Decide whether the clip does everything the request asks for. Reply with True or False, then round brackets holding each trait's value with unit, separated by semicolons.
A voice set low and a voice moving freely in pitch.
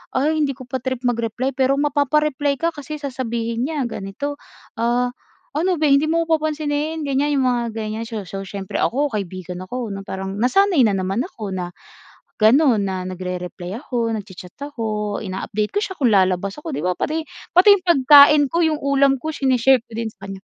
False (250 Hz; 6.1 semitones)